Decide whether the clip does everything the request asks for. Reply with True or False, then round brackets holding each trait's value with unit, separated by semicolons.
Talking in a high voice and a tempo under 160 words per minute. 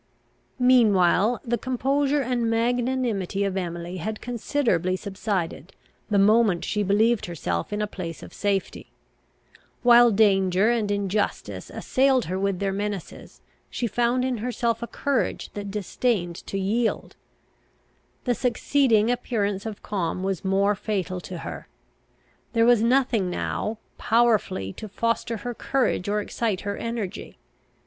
True (210 Hz; 135 wpm)